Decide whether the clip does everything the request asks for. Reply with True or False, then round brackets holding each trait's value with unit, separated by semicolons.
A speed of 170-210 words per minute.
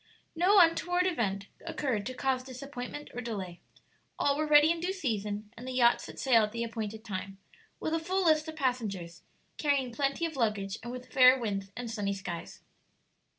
True (185 wpm)